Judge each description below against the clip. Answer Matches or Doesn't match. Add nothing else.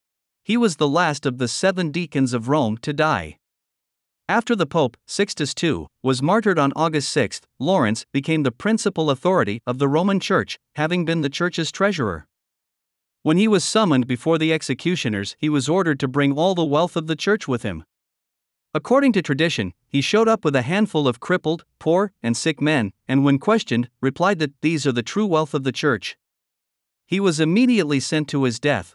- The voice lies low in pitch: Doesn't match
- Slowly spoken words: Doesn't match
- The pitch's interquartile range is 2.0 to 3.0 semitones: Doesn't match